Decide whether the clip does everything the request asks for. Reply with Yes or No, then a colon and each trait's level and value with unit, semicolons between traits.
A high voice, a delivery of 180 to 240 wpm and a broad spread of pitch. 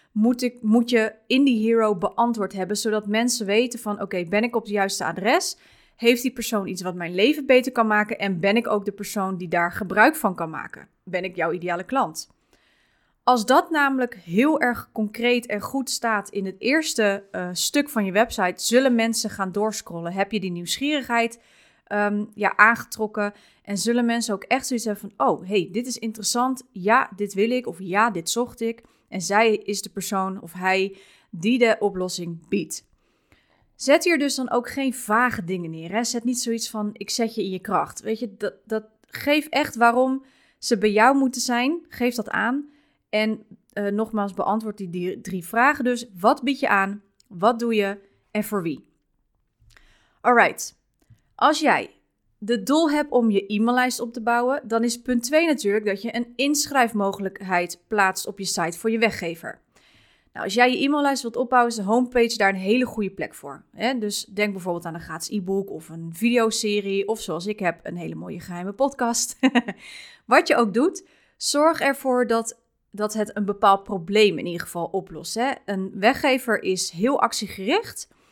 No: high, 220 Hz; average, 190 wpm; average, 3.7 semitones